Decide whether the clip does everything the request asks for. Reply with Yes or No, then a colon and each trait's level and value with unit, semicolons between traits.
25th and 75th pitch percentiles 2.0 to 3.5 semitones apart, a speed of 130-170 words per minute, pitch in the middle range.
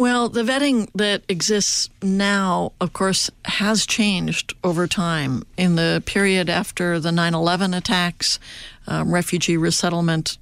Yes: average, 2.8 semitones; slow, 135 wpm; medium, 180 Hz